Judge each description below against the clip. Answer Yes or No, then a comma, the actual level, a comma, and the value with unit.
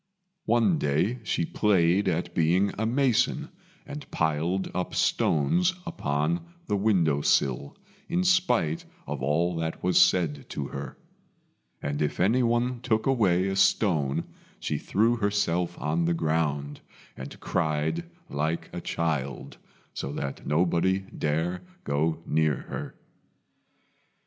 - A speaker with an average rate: No, slow, 125 wpm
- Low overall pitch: Yes, very low, 85 Hz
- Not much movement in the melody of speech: No, wide, 5.6 semitones